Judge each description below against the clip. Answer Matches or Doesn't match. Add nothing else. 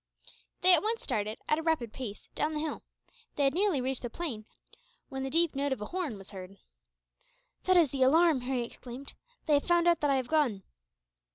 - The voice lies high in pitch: Matches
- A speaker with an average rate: Doesn't match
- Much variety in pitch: Doesn't match